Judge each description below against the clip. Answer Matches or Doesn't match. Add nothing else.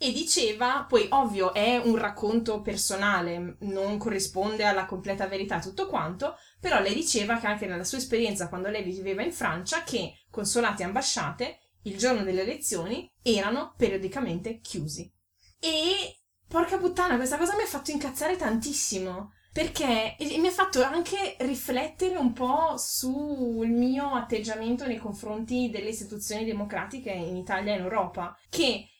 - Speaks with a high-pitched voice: Matches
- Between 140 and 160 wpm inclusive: Matches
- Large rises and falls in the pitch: Matches